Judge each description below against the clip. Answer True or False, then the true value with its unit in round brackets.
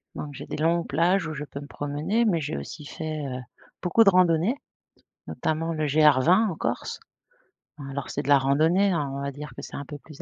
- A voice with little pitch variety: False (3.2 semitones)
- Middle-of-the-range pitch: True (155 Hz)